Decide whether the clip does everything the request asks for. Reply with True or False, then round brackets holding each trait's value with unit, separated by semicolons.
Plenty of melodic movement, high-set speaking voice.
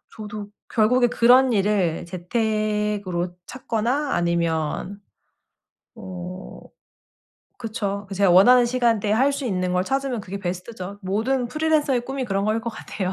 False (4.5 semitones; 210 Hz)